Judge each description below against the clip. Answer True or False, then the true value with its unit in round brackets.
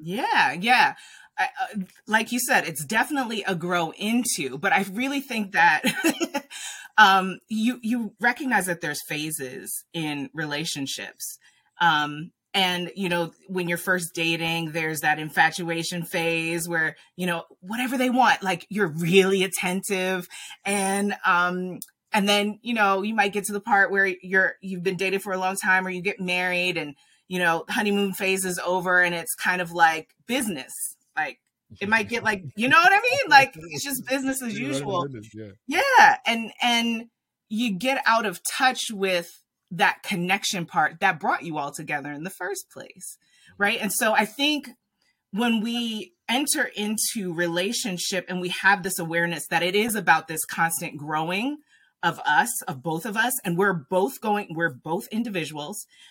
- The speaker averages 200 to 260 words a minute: False (170 wpm)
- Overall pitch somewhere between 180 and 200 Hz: True (190 Hz)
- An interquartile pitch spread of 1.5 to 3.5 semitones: False (4.7 semitones)